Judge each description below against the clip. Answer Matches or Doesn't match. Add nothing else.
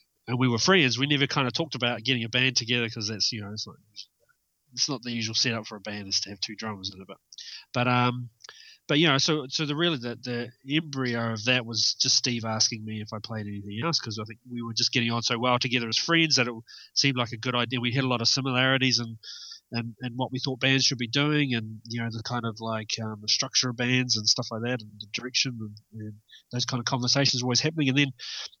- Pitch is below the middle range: Matches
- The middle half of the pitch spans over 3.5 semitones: Doesn't match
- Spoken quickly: Matches